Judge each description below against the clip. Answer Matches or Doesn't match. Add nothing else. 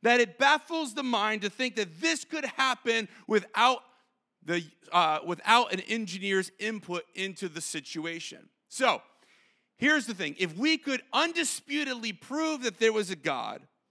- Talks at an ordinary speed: Matches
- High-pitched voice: Matches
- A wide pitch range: Matches